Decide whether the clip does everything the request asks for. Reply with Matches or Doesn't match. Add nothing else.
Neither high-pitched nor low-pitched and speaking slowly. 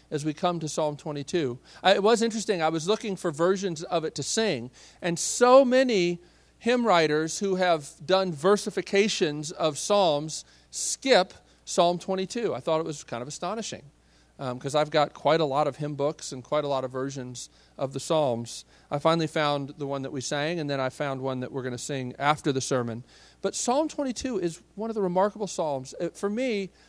Doesn't match